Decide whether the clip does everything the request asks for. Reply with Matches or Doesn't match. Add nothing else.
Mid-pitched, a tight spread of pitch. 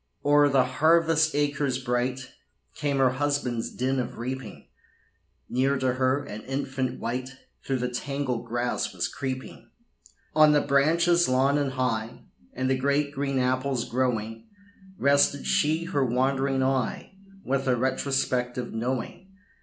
Doesn't match